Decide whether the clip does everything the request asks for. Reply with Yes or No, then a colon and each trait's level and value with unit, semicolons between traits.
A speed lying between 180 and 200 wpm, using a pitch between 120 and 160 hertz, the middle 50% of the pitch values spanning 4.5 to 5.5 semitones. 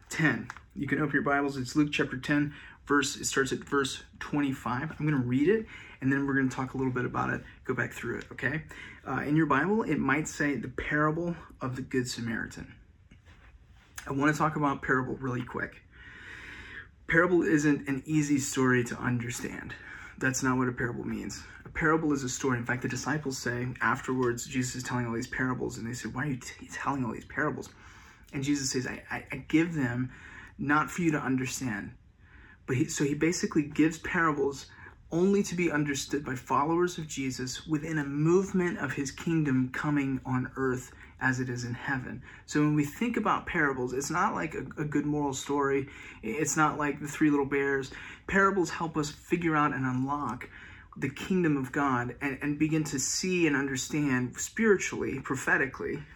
No: average, 195 wpm; medium, 140 Hz; average, 3.2 semitones